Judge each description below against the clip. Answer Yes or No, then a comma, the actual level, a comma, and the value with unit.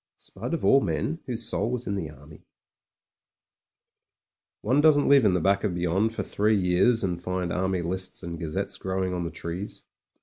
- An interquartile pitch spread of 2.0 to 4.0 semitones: No, average, 4.4 semitones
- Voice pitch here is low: Yes, very low, 95 Hz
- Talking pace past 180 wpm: Yes, average, 190 wpm